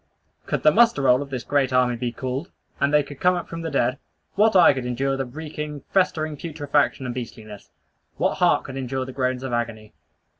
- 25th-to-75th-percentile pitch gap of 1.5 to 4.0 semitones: Yes, average, 3.2 semitones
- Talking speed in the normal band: No, fast, 210 wpm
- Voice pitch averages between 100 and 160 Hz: Yes, low, 135 Hz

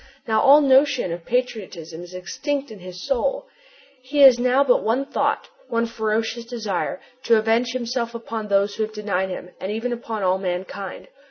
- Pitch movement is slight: No, average, 4.4 semitones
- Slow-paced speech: No, average, 175 wpm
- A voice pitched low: No, high, 225 Hz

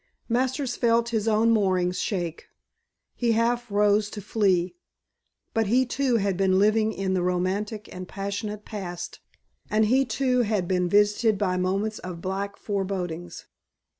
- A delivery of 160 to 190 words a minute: No, average, 145 wpm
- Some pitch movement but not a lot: Yes, average, 3.3 semitones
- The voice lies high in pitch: Yes, high, 205 Hz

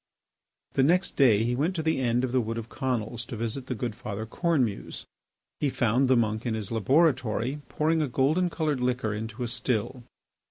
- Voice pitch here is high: No, low, 125 Hz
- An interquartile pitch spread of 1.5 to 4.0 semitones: Yes, average, 3.7 semitones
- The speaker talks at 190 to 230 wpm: Yes, average, 195 wpm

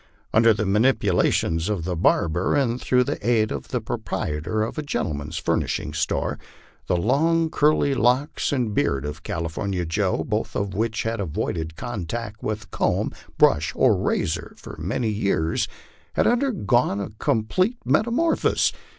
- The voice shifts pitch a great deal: Yes, wide, 6.3 semitones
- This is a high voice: No, low, 105 Hz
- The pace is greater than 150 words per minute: No, average, 145 wpm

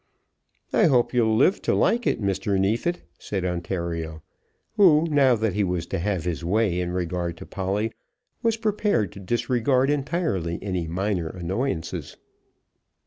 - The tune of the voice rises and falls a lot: Yes, wide, 6.6 semitones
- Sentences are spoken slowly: No, average, 145 wpm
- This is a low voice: Yes, low, 100 Hz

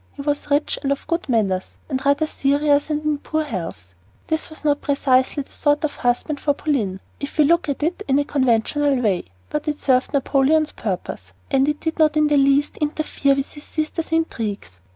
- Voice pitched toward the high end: Yes, very high, 285 Hz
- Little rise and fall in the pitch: Yes, narrow, 2.3 semitones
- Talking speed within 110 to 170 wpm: No, average, 195 wpm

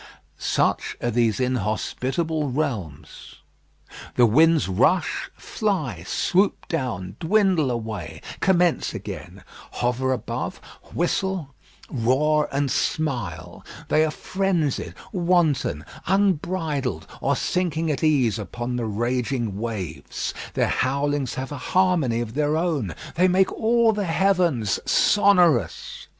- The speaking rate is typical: No, slow, 110 wpm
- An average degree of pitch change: No, wide, 6.6 semitones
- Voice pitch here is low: No, medium, 145 Hz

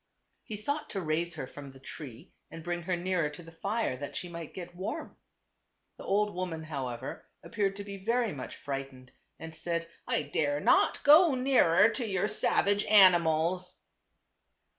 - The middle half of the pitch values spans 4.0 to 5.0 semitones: Yes, average, 4.7 semitones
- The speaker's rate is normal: Yes, average, 165 wpm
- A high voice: No, medium, 175 Hz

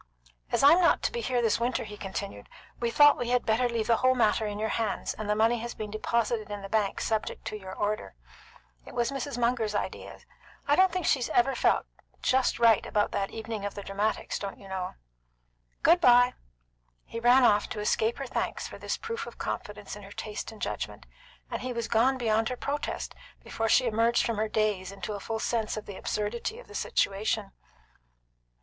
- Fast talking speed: Yes, fast, 210 wpm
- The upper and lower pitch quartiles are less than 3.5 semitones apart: Yes, average, 2.9 semitones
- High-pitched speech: Yes, high, 225 Hz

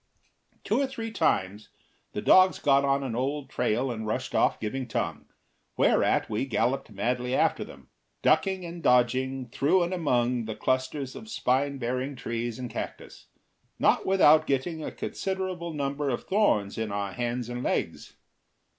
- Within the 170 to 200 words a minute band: No, average, 155 wpm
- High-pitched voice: No, low, 130 Hz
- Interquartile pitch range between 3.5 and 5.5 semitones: Yes, average, 4.6 semitones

